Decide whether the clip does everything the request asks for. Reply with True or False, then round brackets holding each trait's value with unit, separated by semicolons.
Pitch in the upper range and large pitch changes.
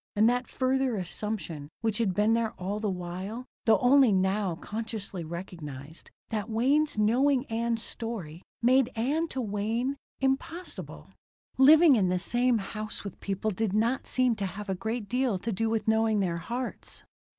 False (220 Hz; 4.1 semitones)